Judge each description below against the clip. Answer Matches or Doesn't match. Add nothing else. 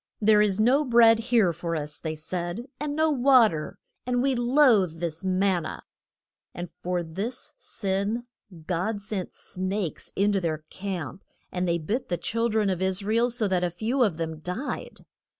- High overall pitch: Matches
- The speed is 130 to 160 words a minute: Doesn't match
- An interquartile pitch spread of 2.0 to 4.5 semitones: Doesn't match